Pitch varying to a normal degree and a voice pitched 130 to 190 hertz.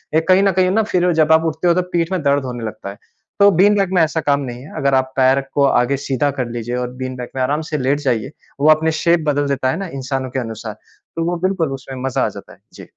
Yes: average, 4.5 semitones; medium, 140 Hz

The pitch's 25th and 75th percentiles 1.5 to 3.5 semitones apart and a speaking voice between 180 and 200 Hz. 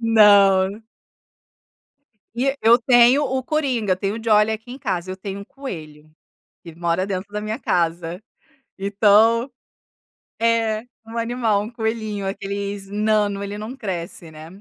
No: average, 3.0 semitones; high, 210 Hz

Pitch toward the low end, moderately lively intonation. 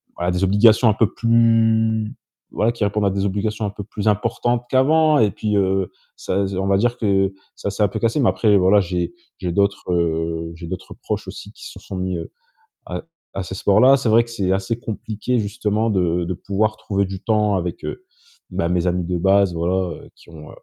Yes: low, 100 Hz; average, 3.3 semitones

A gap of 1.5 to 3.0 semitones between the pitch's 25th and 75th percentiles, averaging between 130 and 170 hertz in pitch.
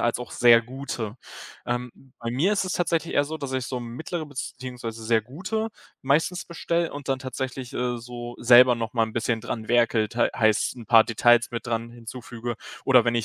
No: narrow, 2.6 semitones; low, 120 Hz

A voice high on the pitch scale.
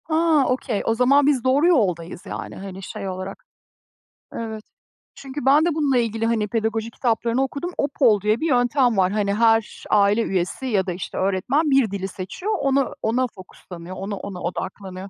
Yes: high, 225 Hz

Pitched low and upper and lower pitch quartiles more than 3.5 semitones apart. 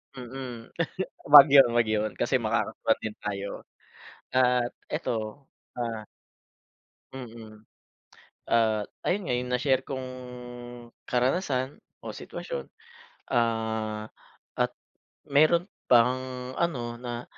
No: low, 125 Hz; average, 2.9 semitones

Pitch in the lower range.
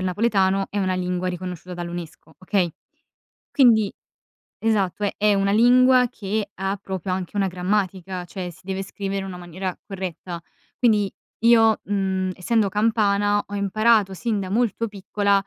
No: high, 195 Hz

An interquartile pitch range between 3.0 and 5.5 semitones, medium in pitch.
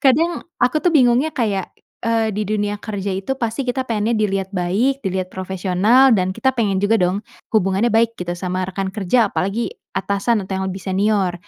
No: average, 3.8 semitones; high, 205 Hz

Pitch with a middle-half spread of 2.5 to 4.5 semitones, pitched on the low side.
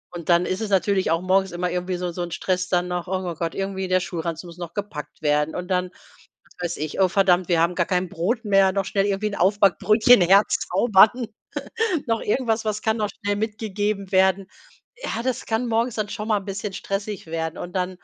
No: average, 2.8 semitones; high, 190 Hz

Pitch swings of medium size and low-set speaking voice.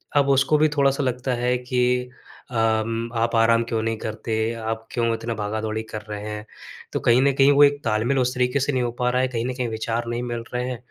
No: narrow, 2.2 semitones; low, 120 Hz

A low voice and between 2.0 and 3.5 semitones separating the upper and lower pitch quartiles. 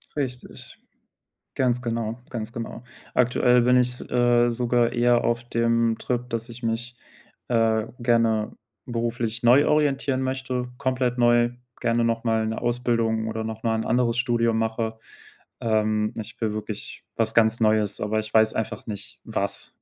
No: low, 115 Hz; narrow, 1.5 semitones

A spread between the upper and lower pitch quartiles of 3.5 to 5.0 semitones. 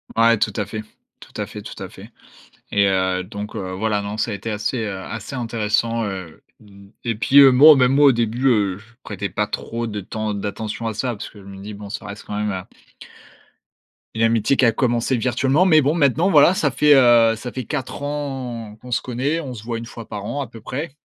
Yes: average, 4.0 semitones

